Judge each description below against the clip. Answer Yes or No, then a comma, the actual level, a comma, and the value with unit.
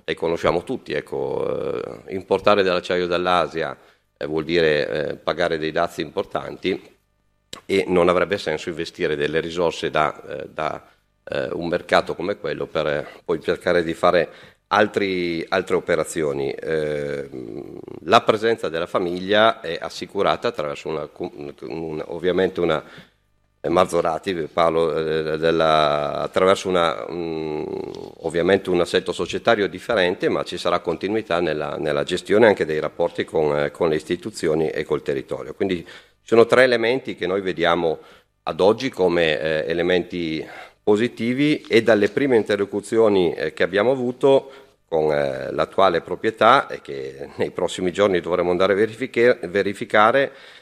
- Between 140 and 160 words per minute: No, average, 130 wpm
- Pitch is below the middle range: Yes, low, 100 Hz